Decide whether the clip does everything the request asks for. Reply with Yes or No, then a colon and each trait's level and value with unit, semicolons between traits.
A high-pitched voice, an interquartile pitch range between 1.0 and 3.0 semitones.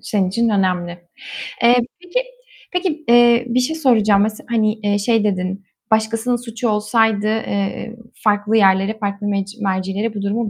Yes: high, 215 Hz; average, 2.7 semitones